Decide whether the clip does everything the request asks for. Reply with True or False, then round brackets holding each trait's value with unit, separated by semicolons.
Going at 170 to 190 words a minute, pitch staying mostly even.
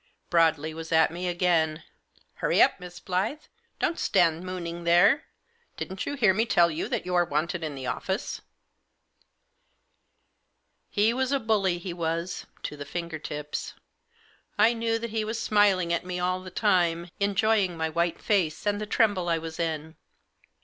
False (175 wpm; 3.8 semitones)